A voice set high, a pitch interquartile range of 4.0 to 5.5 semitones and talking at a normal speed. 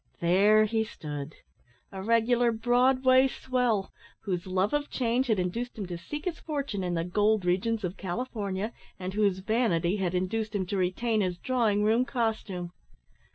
Yes: high, 210 Hz; average, 4.5 semitones; average, 160 wpm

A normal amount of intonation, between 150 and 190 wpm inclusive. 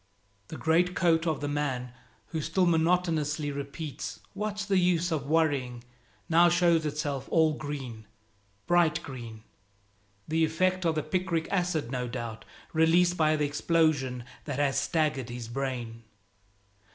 No: average, 3.7 semitones; slow, 135 wpm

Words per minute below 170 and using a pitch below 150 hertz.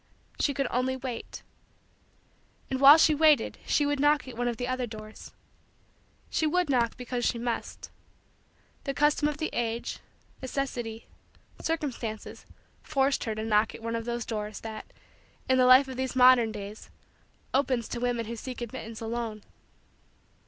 No: average, 160 wpm; high, 245 Hz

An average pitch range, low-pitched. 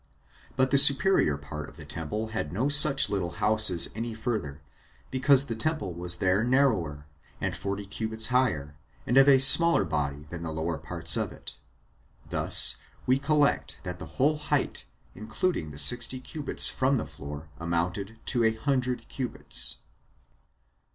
No: wide, 7.9 semitones; low, 110 Hz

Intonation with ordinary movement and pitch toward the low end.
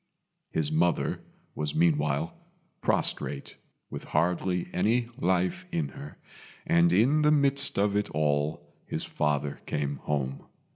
No: wide, 6.8 semitones; very low, 85 Hz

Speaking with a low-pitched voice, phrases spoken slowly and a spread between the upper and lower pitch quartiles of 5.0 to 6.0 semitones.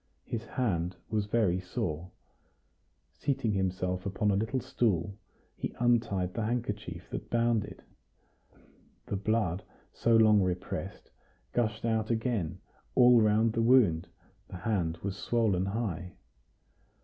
No: low, 105 Hz; slow, 125 wpm; average, 3.9 semitones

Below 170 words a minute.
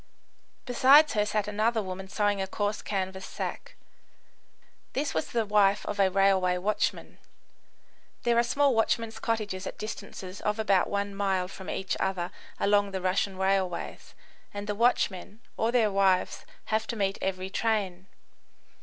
Yes: average, 150 wpm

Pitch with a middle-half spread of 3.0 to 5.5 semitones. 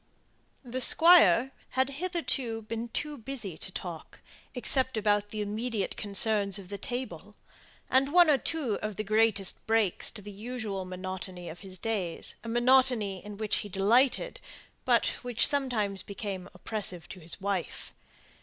Yes: average, 4.3 semitones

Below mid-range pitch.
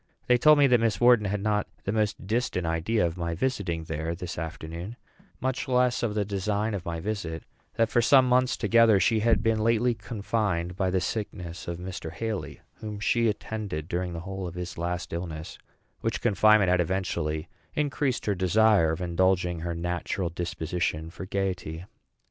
Yes: very low, 95 Hz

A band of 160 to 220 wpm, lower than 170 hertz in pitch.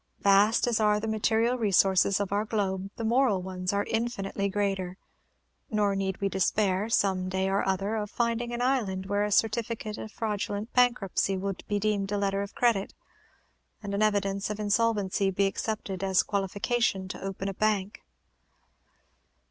No: average, 165 wpm; high, 205 Hz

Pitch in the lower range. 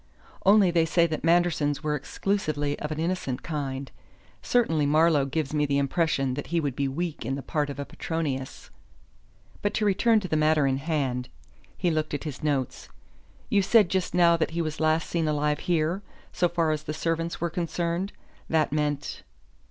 No: medium, 155 Hz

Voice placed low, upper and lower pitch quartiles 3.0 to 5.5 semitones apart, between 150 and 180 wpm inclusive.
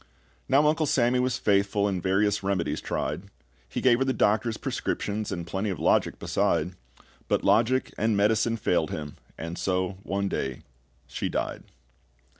Yes: low, 100 Hz; average, 3.7 semitones; average, 155 wpm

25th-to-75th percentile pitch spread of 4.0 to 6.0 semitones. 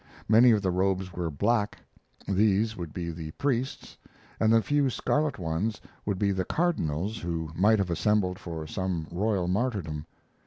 Yes: average, 4.4 semitones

